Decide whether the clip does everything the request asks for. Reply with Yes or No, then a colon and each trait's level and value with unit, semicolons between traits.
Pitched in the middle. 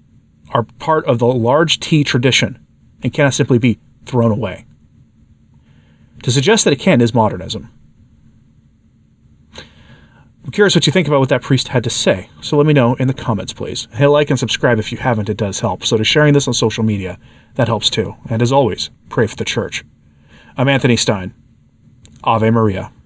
No: low, 120 Hz